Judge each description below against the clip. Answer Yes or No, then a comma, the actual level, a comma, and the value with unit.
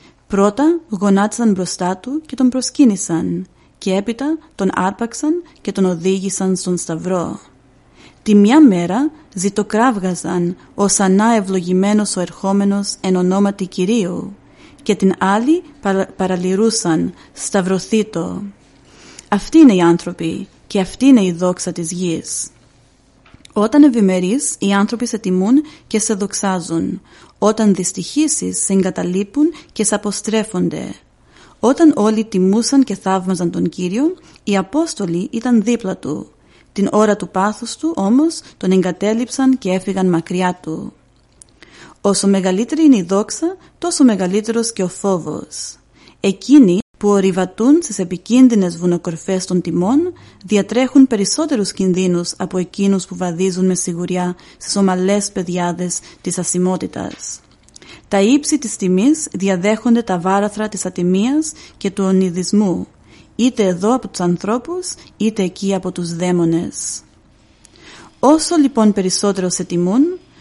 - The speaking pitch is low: No, high, 195 Hz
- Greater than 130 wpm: No, average, 125 wpm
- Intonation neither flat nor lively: Yes, average, 4.1 semitones